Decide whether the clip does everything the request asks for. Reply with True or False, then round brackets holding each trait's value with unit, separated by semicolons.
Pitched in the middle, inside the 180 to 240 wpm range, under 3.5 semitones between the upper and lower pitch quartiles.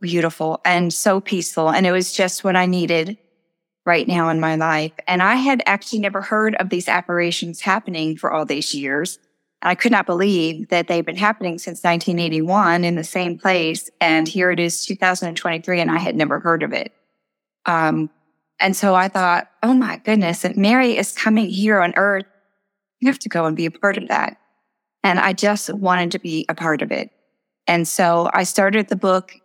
True (180 Hz; 200 wpm; 3.1 semitones)